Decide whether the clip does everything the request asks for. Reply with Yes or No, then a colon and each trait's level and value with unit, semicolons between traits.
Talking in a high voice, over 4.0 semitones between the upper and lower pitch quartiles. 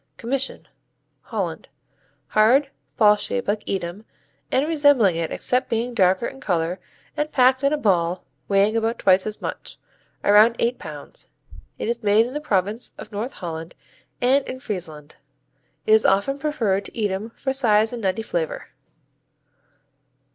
Yes: high, 220 Hz; average, 5.0 semitones